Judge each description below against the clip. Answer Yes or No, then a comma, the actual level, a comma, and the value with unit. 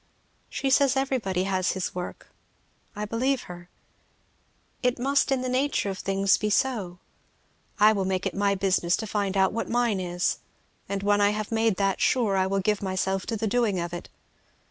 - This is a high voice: Yes, high, 200 Hz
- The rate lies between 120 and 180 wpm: No, average, 190 wpm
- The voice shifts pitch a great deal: No, average, 3.6 semitones